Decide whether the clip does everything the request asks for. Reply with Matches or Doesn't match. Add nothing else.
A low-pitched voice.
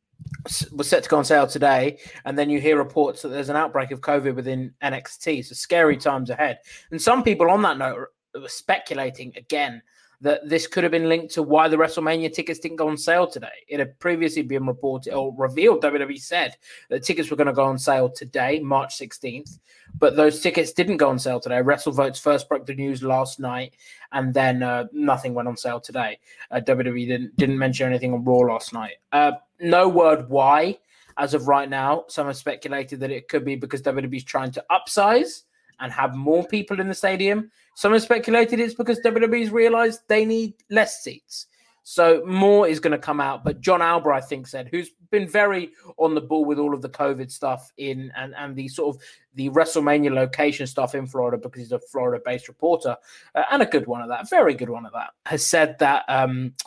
Doesn't match